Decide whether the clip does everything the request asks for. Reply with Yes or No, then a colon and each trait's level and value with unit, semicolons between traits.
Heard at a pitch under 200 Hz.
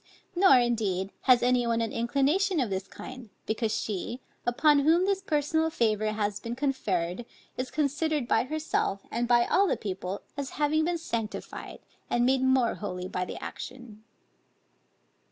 No: high, 245 Hz